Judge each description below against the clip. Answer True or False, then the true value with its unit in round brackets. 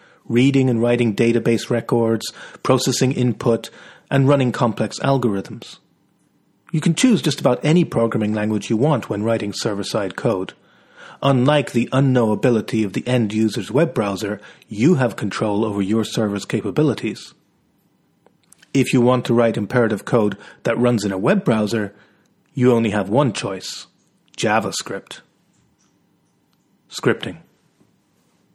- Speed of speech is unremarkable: False (130 wpm)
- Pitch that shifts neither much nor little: True (3.1 semitones)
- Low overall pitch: True (120 Hz)